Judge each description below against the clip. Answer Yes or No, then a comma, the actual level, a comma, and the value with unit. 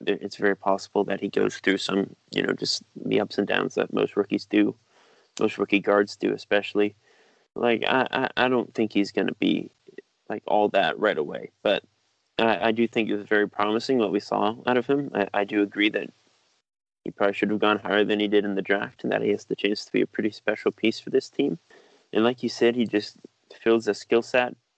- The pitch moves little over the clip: Yes, narrow, 2.3 semitones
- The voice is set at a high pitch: No, low, 105 Hz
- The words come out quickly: Yes, fast, 230 wpm